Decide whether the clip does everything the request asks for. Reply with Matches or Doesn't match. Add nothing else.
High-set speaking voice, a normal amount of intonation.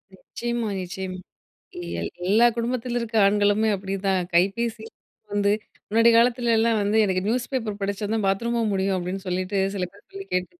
Matches